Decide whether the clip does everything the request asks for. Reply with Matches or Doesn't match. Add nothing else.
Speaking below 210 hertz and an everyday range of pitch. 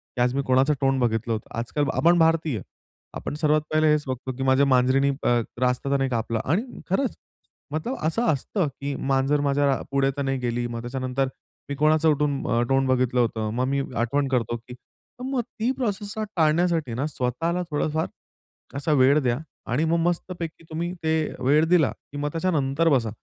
Matches